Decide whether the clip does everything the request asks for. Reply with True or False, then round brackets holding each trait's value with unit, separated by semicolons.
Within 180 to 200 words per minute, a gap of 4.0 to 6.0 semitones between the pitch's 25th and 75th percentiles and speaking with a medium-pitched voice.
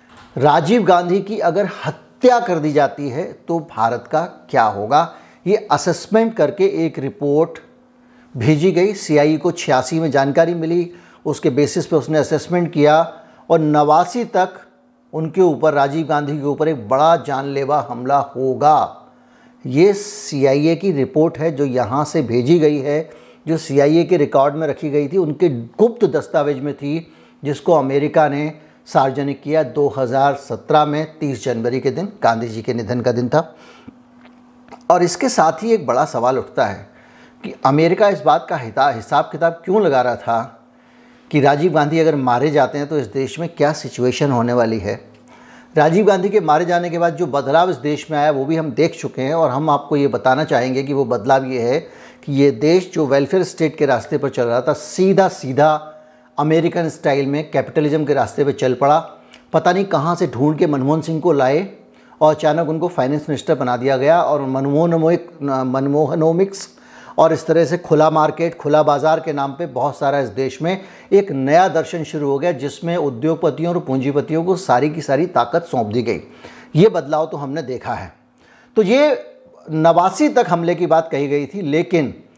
False (185 wpm; 3.5 semitones; 155 Hz)